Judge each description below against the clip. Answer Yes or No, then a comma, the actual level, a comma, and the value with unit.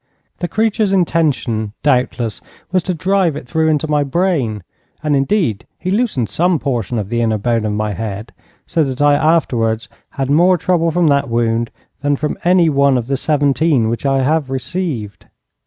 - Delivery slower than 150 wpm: No, average, 175 wpm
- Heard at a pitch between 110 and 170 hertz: Yes, medium, 140 Hz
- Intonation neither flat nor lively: No, wide, 6.1 semitones